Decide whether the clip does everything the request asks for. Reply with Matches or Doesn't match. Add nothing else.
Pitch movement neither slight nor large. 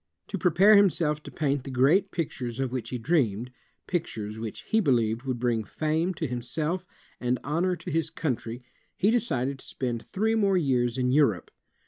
Doesn't match